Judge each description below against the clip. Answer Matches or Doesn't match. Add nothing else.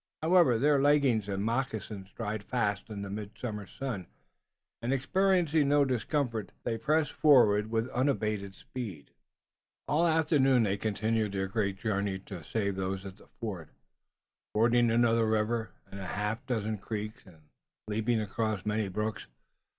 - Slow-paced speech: Doesn't match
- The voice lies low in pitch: Matches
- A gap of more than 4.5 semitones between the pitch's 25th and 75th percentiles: Doesn't match